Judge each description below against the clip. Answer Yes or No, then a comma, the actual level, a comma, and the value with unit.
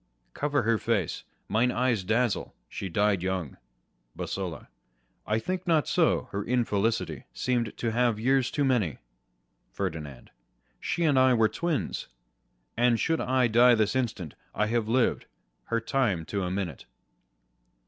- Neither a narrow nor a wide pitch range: Yes, average, 4.2 semitones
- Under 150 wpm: Yes, average, 140 wpm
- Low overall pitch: Yes, low, 115 Hz